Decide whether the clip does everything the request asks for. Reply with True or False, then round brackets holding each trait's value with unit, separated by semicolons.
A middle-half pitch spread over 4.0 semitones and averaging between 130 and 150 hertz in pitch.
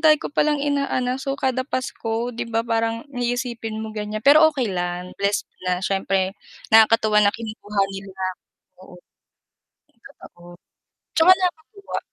False (5.0 semitones; 225 Hz)